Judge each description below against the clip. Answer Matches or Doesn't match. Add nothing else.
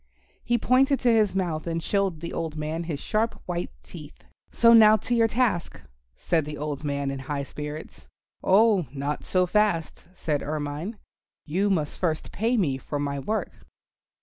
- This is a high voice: Doesn't match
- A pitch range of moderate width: Doesn't match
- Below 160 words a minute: Doesn't match